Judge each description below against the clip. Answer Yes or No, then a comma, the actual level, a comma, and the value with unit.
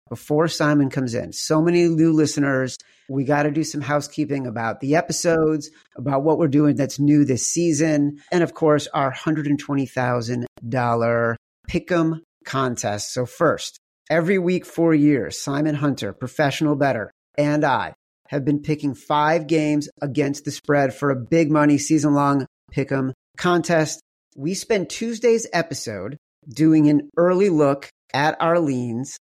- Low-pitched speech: No, medium, 150 Hz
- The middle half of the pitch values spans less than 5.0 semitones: Yes, average, 2.7 semitones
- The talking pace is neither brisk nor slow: Yes, average, 150 wpm